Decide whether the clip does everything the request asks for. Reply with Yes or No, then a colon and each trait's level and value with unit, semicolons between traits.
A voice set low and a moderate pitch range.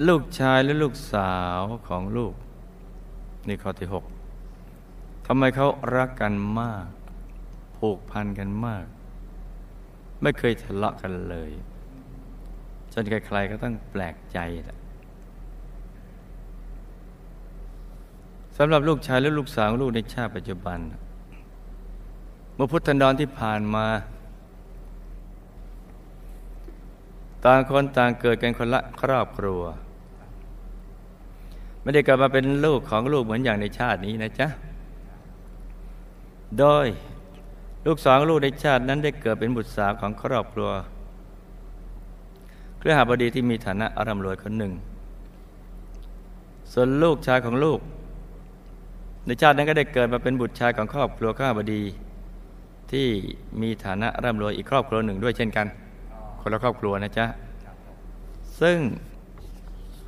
Yes: low, 110 Hz; average, 4.9 semitones